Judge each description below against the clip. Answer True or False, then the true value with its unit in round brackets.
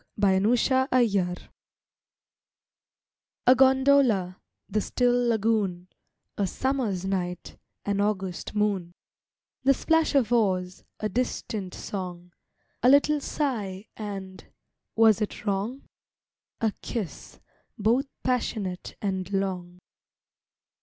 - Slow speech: True (95 wpm)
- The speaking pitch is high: True (210 Hz)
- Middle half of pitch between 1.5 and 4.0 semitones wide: False (4.6 semitones)